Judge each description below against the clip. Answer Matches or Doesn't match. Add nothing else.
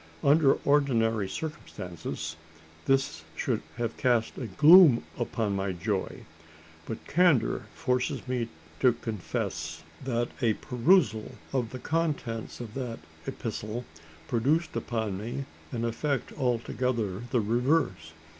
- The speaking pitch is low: Matches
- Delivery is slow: Matches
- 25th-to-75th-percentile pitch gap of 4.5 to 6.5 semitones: Doesn't match